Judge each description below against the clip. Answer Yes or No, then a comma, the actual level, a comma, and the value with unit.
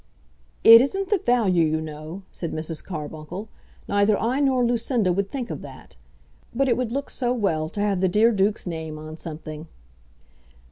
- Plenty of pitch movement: Yes, wide, 7.1 semitones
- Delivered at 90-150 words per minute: No, average, 175 wpm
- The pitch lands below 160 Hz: No, high, 200 Hz